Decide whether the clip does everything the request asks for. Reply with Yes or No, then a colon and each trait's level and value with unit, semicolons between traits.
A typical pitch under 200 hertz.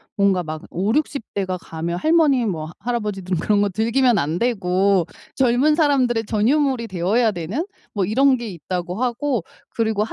No: high, 215 Hz